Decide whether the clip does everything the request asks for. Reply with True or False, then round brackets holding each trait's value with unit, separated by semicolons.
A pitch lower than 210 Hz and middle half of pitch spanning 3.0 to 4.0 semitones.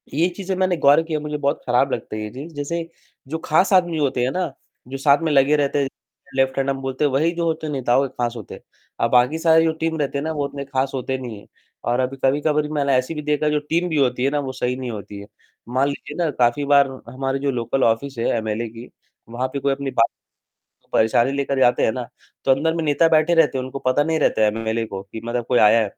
True (135 Hz; 3.5 semitones)